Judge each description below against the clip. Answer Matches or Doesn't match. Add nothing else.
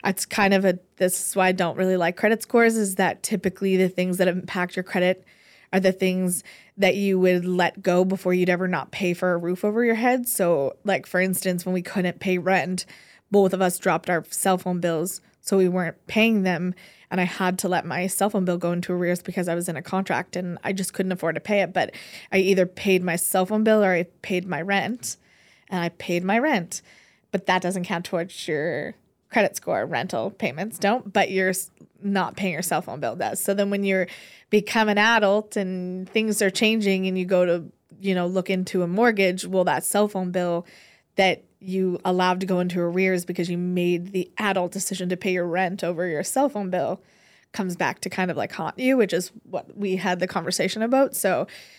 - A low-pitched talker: Doesn't match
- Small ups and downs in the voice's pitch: Matches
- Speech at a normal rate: Doesn't match